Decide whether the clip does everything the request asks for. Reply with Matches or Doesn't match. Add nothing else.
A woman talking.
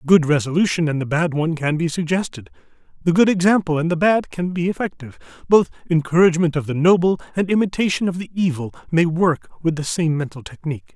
Doesn't match